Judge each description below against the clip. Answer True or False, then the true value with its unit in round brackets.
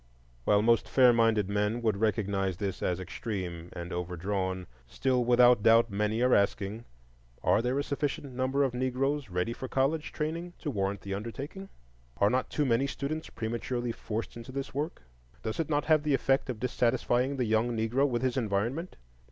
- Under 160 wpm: False (175 wpm)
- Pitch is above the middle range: False (120 Hz)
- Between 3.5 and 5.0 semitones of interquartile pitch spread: True (4.6 semitones)